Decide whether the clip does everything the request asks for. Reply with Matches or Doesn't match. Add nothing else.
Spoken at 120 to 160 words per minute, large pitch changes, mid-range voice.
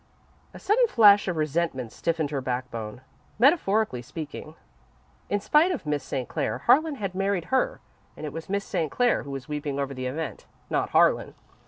Doesn't match